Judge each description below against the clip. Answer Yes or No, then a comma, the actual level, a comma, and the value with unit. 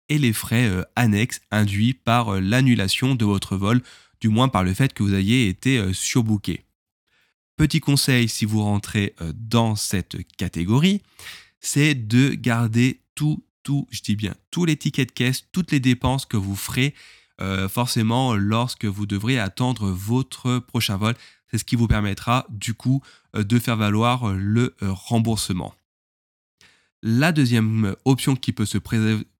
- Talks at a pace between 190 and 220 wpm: No, average, 155 wpm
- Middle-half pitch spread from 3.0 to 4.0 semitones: Yes, average, 3.6 semitones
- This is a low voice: Yes, low, 115 Hz